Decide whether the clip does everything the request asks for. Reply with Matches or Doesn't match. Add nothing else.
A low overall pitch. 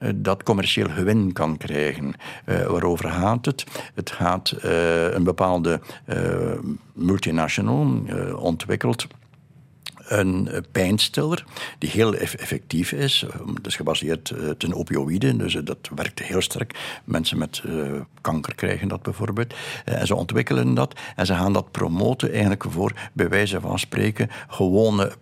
Matches